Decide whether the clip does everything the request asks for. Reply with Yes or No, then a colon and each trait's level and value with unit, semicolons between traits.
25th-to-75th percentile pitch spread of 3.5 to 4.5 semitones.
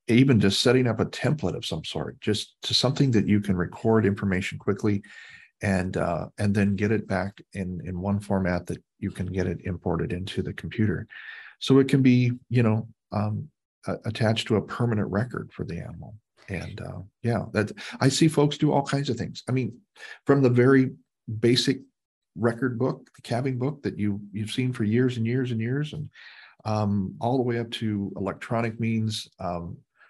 Yes: average, 4.1 semitones